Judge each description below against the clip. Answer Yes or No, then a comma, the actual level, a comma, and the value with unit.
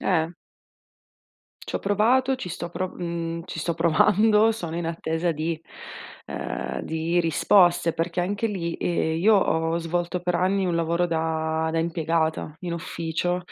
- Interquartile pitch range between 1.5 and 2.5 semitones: Yes, narrow, 1.8 semitones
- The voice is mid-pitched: Yes, medium, 170 Hz